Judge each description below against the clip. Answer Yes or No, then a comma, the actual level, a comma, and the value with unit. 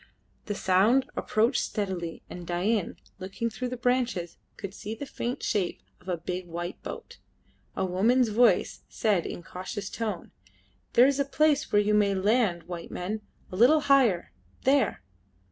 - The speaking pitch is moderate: No, high, 210 Hz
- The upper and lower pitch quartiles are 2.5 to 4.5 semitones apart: No, average, 5.2 semitones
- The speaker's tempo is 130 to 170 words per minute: Yes, average, 160 wpm